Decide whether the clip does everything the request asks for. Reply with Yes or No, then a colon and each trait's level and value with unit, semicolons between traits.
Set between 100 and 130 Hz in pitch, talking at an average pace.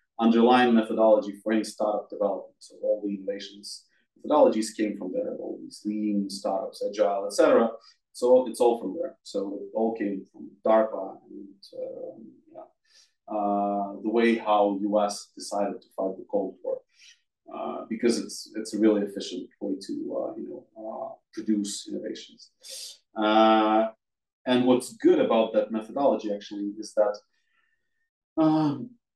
Yes: low, 110 Hz; average, 145 wpm